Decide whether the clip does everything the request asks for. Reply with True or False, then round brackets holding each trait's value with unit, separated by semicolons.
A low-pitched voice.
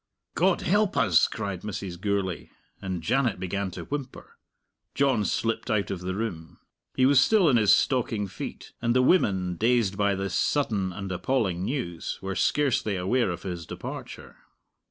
True (100 Hz)